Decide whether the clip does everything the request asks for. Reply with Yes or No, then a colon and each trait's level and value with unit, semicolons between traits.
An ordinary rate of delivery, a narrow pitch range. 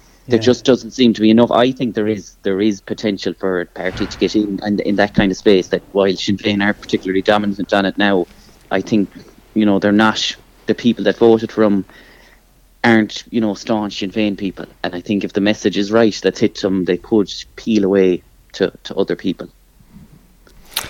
No: fast, 215 wpm; narrow, 1.9 semitones